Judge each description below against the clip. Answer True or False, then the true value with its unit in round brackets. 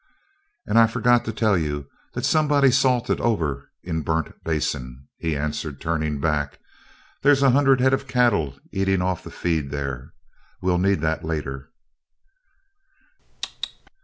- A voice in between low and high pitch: False (85 Hz)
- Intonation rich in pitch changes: True (8.2 semitones)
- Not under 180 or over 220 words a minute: False (135 wpm)